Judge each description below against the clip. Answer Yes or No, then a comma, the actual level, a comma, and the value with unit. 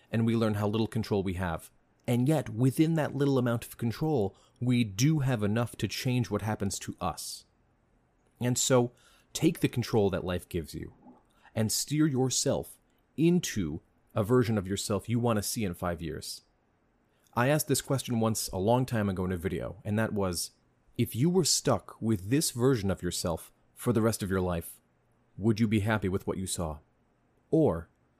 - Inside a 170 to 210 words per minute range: Yes, average, 190 wpm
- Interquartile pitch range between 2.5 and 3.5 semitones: No, average, 4.4 semitones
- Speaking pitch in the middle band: No, low, 115 Hz